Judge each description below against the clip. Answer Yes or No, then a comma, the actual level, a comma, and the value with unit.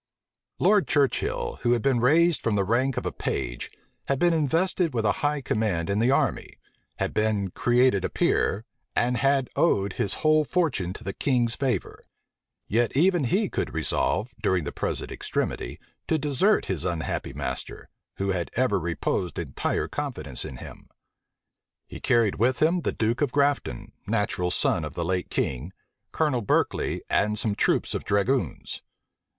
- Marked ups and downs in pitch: Yes, wide, 6.8 semitones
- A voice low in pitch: Yes, low, 120 Hz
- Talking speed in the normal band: Yes, average, 160 wpm